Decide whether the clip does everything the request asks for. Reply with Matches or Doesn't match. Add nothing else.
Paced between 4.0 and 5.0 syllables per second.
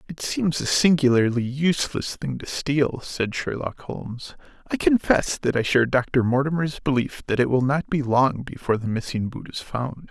Matches